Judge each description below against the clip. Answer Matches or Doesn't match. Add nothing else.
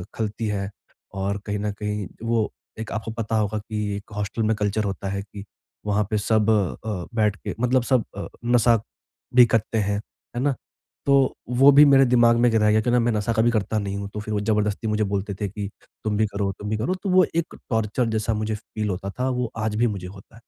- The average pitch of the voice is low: Matches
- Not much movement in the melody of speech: Matches